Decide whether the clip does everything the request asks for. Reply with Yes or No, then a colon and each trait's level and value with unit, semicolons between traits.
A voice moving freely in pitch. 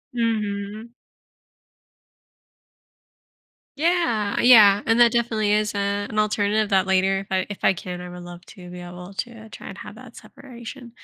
No: average, 3.0 semitones